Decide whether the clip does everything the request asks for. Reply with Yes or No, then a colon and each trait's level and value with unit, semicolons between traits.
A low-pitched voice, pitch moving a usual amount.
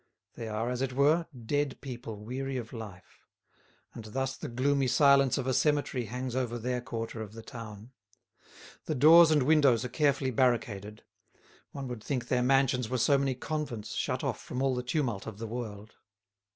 Yes: low, 125 Hz; average, 3.2 semitones